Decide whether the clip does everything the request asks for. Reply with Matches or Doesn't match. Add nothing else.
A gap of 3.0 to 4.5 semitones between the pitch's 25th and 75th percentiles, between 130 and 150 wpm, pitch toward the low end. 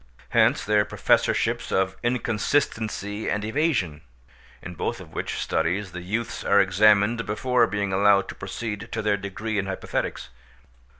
Doesn't match